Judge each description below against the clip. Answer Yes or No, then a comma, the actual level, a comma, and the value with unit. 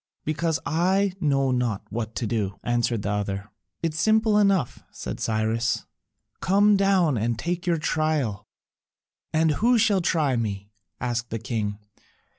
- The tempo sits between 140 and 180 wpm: Yes, average, 145 wpm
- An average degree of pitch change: No, wide, 8.0 semitones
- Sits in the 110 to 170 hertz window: Yes, low, 135 Hz